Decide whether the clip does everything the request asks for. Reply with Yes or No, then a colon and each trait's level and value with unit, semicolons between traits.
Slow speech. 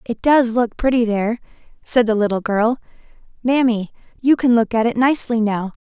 No: average, 175 wpm